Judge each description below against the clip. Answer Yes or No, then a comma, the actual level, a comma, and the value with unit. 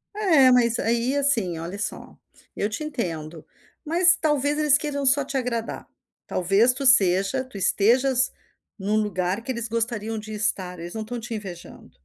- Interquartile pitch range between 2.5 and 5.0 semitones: No, wide, 5.4 semitones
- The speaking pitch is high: Yes, high, 230 Hz